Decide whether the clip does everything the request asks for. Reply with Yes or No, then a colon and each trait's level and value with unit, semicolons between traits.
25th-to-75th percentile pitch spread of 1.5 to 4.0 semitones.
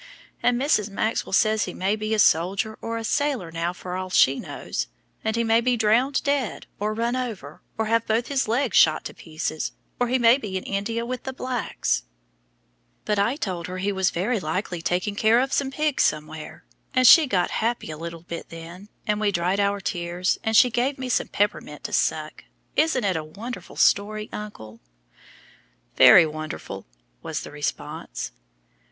No: average, 5.0 semitones